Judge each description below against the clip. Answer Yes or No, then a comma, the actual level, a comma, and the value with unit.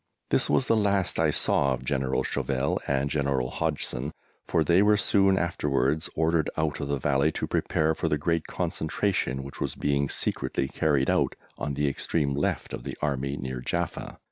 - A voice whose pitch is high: No, very low, 70 Hz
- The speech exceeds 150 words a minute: Yes, average, 180 wpm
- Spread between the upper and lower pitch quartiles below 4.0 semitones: Yes, average, 2.9 semitones